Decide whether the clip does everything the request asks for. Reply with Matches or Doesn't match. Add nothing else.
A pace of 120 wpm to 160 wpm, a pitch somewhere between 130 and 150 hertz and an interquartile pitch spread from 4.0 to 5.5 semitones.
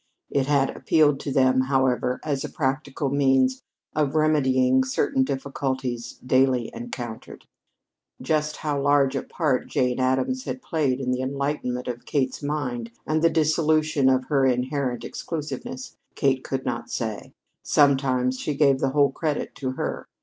Doesn't match